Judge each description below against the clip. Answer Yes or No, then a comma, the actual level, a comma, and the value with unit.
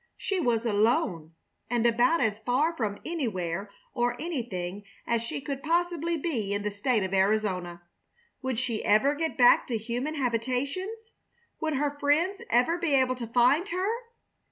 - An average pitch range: No, wide, 6.2 semitones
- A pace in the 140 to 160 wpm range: Yes, average, 155 wpm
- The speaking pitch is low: No, high, 245 Hz